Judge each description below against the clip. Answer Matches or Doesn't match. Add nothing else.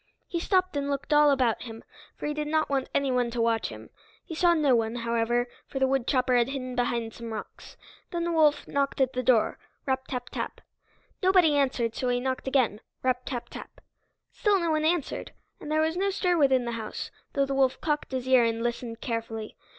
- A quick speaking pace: Matches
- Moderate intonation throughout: Matches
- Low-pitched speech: Doesn't match